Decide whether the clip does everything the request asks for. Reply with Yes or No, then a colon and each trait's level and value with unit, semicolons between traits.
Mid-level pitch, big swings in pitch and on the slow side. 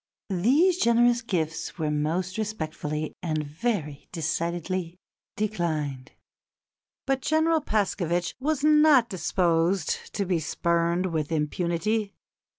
Yes: medium, 175 Hz; wide, 5.8 semitones; slow, 100 wpm